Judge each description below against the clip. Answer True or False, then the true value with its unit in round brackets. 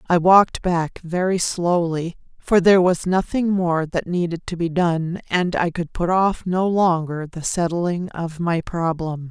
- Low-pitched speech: False (175 Hz)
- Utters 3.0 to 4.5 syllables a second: True (4.1 syllables/s)